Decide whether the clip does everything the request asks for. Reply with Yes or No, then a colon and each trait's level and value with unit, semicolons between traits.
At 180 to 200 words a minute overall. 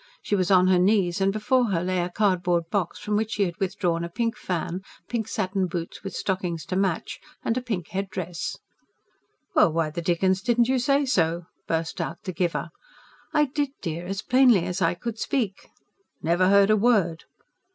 Yes: average, 195 wpm